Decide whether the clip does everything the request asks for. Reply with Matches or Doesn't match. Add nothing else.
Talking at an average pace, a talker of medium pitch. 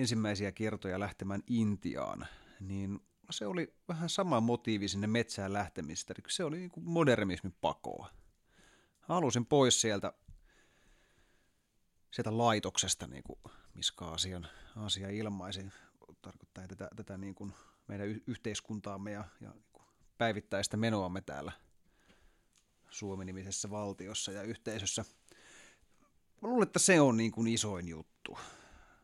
Doesn't match